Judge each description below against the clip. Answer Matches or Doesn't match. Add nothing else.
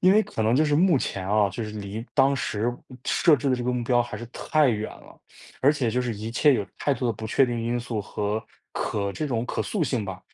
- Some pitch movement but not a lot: Matches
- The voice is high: Doesn't match